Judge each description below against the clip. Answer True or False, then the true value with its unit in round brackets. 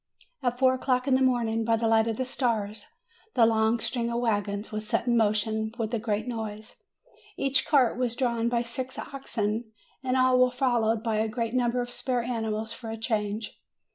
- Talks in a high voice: True (230 Hz)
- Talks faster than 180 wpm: True (200 wpm)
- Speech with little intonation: True (2.2 semitones)